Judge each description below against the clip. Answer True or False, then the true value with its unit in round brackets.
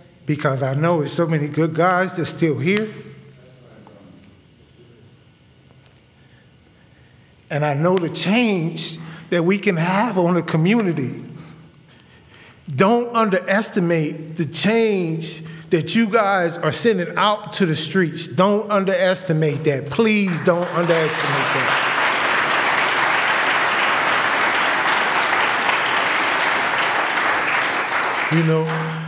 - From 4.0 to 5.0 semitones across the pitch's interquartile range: False (3.3 semitones)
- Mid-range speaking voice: True (170 Hz)